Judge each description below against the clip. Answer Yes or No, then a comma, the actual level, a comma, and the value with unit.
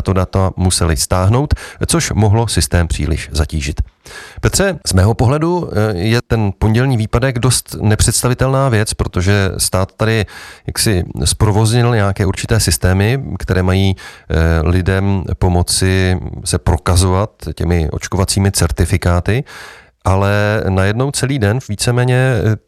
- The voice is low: Yes, low, 100 Hz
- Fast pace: No, slow, 115 wpm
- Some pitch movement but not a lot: Yes, average, 3.6 semitones